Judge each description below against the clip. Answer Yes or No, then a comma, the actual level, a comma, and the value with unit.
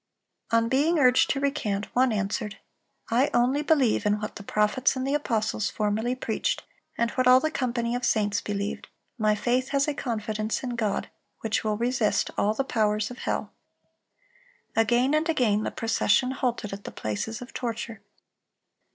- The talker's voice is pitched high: Yes, high, 235 Hz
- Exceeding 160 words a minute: Yes, average, 170 wpm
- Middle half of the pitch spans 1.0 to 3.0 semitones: No, average, 3.5 semitones